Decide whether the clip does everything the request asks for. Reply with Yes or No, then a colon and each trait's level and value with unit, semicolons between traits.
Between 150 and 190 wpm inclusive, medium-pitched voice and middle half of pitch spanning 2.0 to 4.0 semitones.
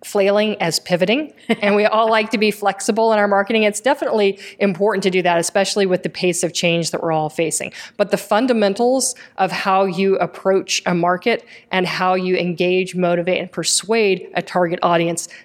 No: average, 185 wpm; high, 195 Hz; average, 2.8 semitones